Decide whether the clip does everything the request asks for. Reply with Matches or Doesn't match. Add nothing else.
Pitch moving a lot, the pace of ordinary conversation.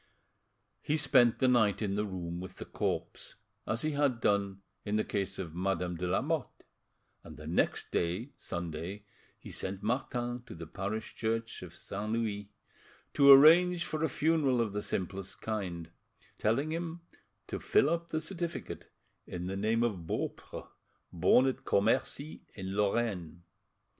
Matches